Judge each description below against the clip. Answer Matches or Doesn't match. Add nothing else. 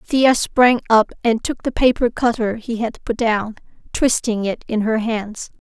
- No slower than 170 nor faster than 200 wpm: Matches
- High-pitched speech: Matches